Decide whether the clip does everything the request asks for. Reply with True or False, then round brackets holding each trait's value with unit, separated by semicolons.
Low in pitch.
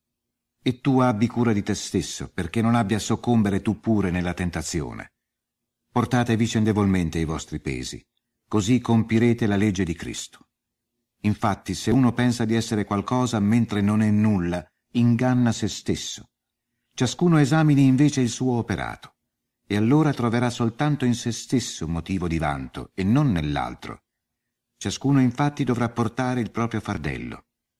True (115 Hz)